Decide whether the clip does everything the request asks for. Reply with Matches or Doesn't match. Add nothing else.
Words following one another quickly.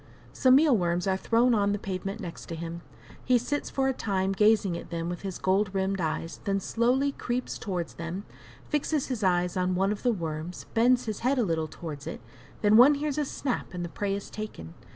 Matches